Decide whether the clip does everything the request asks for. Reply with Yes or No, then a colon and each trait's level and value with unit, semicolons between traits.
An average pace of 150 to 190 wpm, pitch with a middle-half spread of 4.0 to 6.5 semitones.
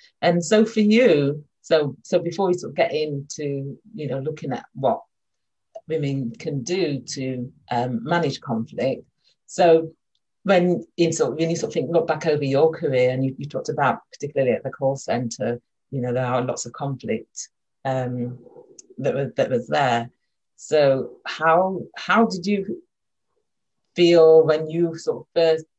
Yes: average, 170 wpm; average, 4.6 semitones